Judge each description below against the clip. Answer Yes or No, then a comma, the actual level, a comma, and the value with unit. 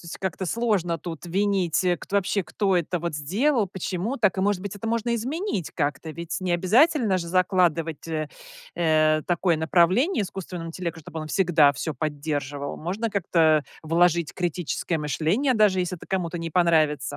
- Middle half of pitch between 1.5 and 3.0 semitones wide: No, average, 3.6 semitones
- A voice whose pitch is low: No, medium, 175 Hz